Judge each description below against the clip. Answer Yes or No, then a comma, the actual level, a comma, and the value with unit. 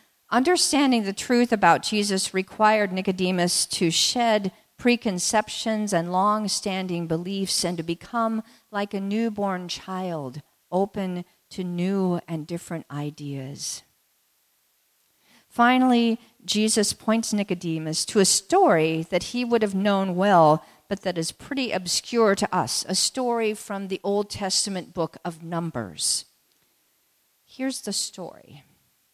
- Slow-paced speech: Yes, slow, 120 wpm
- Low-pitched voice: No, high, 195 Hz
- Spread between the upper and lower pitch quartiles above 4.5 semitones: No, average, 4.0 semitones